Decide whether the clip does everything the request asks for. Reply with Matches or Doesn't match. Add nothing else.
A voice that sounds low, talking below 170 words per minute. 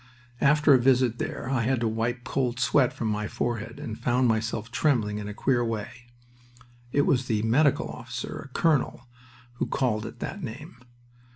Doesn't match